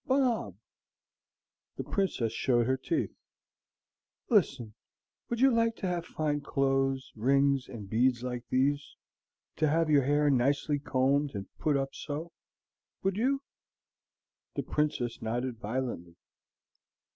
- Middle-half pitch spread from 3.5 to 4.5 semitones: Yes, average, 3.8 semitones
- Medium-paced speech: No, slow, 120 wpm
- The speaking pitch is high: No, medium, 140 Hz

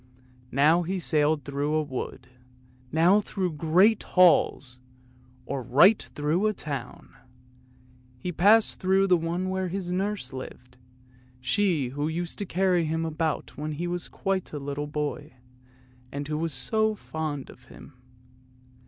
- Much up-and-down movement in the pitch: No, average, 4.3 semitones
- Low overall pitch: No, medium, 160 Hz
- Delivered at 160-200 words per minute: No, average, 145 wpm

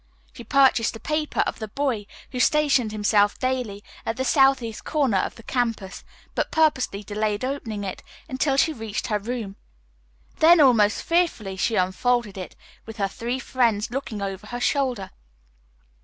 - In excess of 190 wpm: No, average, 155 wpm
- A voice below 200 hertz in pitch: No, high, 230 Hz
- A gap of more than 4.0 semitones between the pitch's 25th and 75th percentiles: Yes, average, 4.4 semitones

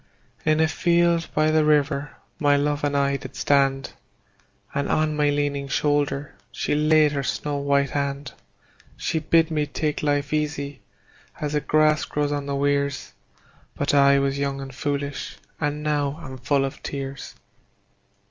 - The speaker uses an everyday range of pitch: No, narrow, 1.4 semitones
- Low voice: No, medium, 145 Hz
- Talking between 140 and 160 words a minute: Yes, average, 155 wpm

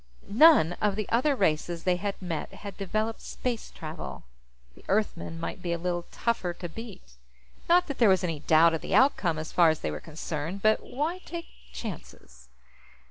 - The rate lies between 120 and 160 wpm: No, average, 185 wpm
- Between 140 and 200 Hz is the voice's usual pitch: Yes, medium, 185 Hz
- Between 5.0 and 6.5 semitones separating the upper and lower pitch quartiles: Yes, wide, 5.6 semitones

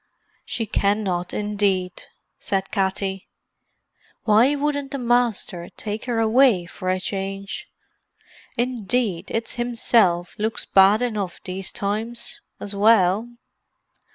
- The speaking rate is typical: No, slow, 105 wpm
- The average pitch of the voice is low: No, high, 210 Hz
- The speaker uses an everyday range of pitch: Yes, average, 3.7 semitones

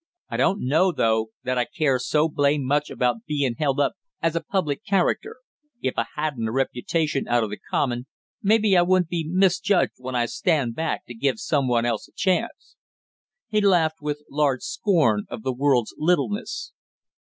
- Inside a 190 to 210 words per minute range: No, average, 180 wpm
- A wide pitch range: Yes, wide, 5.7 semitones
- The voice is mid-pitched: Yes, medium, 150 Hz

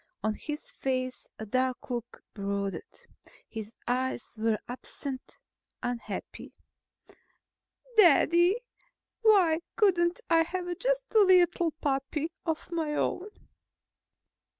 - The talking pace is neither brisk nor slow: No, slow, 100 wpm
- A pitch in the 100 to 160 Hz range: No, very high, 300 Hz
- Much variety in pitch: Yes, wide, 6.2 semitones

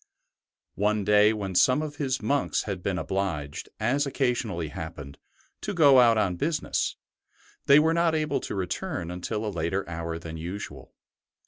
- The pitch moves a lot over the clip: Yes, wide, 7.7 semitones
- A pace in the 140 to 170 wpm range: Yes, average, 155 wpm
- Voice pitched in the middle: No, low, 105 Hz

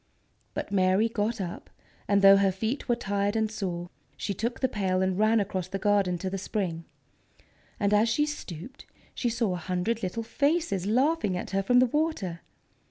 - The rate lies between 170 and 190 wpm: Yes, average, 185 wpm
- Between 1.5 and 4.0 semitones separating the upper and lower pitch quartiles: Yes, average, 3.7 semitones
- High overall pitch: Yes, high, 205 Hz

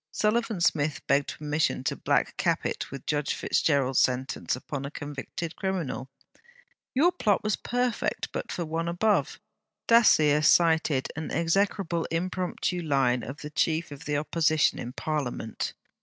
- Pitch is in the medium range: Yes, medium, 155 Hz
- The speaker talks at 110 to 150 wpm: Yes, average, 140 wpm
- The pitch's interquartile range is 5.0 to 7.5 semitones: No, average, 4.0 semitones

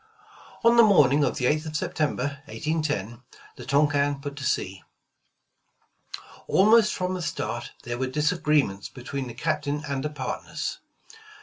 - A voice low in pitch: No, medium, 145 Hz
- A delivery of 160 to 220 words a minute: No, average, 150 wpm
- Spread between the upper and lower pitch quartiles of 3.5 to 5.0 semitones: No, average, 2.7 semitones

